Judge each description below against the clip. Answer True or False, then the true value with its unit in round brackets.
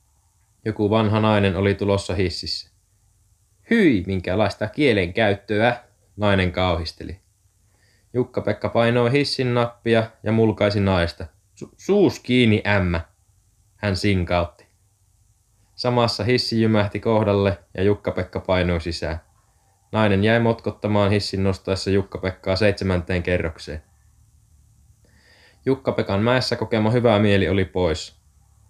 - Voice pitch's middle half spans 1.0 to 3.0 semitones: True (2.4 semitones)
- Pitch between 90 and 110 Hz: True (100 Hz)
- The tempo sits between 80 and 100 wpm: True (95 wpm)